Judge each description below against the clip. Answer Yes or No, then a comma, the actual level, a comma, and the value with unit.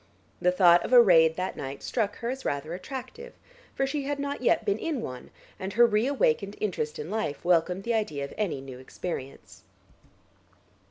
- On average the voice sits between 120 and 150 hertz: No, high, 195 Hz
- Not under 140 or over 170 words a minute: No, average, 185 wpm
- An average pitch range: No, wide, 7.0 semitones